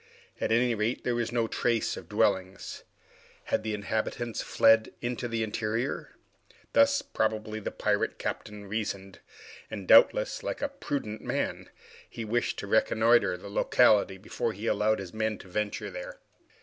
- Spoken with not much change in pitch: Yes, narrow, 2.2 semitones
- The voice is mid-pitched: No, low, 110 Hz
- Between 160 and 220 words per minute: No, average, 150 wpm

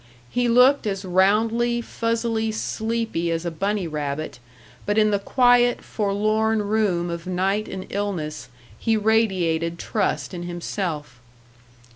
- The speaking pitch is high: Yes, high, 205 Hz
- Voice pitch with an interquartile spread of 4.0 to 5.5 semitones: Yes, average, 4.3 semitones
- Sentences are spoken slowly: Yes, slow, 125 wpm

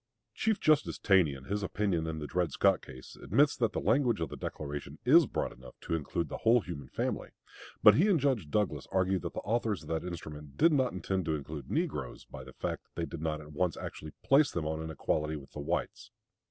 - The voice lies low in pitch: Yes, very low, 85 Hz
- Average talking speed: No, fast, 230 wpm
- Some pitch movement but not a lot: No, wide, 6.7 semitones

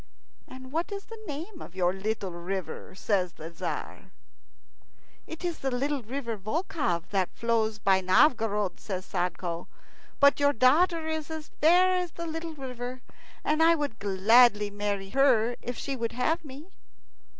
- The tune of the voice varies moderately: No, wide, 7.7 semitones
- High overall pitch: Yes, high, 245 Hz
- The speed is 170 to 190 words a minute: No, average, 155 wpm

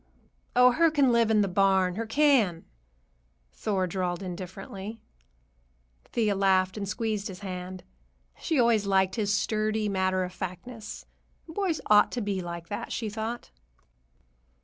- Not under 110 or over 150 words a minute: Yes, average, 140 wpm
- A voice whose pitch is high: Yes, high, 205 Hz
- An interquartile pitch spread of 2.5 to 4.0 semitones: Yes, average, 3.4 semitones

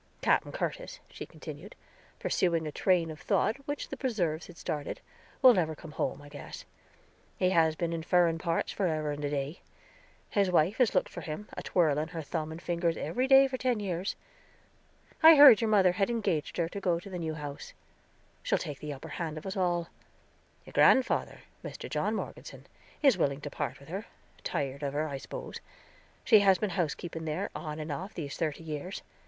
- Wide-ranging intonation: No, average, 4.3 semitones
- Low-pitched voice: No, medium, 170 Hz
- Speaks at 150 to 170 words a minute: No, average, 195 wpm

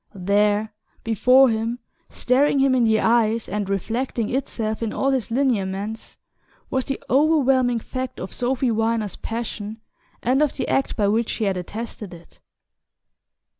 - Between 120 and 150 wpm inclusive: Yes, average, 145 wpm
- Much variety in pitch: No, average, 3.4 semitones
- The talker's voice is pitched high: Yes, high, 230 Hz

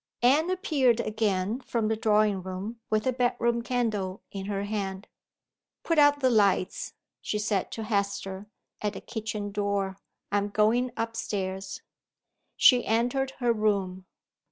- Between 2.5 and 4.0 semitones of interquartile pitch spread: Yes, average, 3.1 semitones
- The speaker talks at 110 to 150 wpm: Yes, average, 145 wpm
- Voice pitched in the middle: No, high, 215 Hz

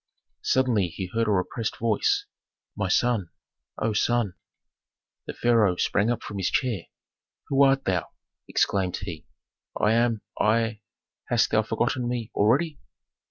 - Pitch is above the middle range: No, low, 115 Hz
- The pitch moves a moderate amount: Yes, average, 3.6 semitones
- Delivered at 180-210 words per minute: No, slow, 135 wpm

